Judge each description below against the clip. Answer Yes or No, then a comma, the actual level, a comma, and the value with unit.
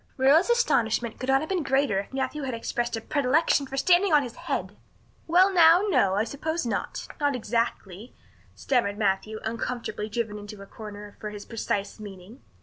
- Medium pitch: No, high, 240 Hz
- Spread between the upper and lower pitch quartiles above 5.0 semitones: Yes, wide, 5.4 semitones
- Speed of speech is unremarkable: Yes, average, 175 wpm